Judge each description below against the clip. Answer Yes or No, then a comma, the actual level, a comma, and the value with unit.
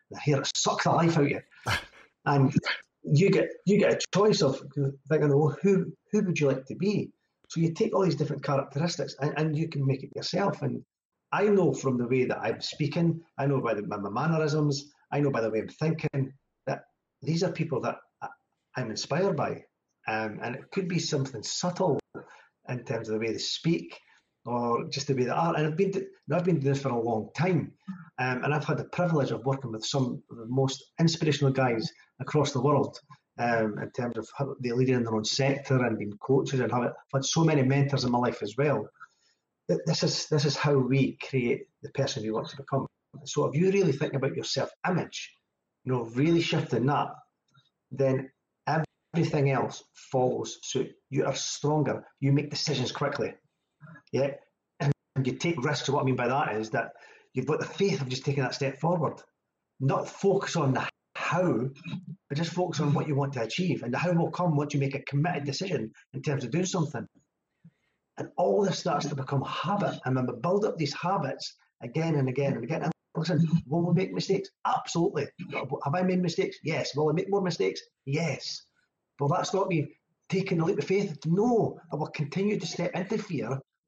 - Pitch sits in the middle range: Yes, medium, 145 Hz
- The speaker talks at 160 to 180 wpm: No, fast, 205 wpm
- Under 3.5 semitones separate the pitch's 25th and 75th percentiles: No, average, 3.8 semitones